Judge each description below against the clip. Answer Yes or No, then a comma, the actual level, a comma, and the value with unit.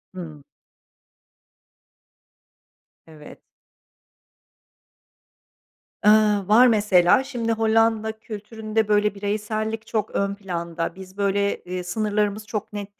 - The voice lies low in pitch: No, high, 210 Hz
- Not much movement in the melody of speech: Yes, narrow, 2.1 semitones